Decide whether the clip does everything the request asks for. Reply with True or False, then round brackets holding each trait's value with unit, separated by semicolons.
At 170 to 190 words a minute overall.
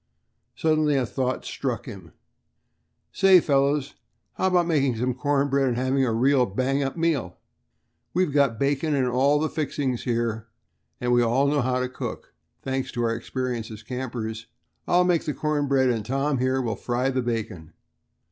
True (175 wpm)